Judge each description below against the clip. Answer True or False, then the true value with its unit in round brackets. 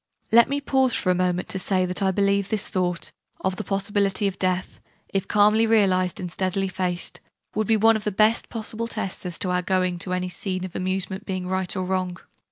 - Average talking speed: False (215 wpm)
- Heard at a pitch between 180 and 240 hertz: True (190 Hz)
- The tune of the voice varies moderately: False (2.3 semitones)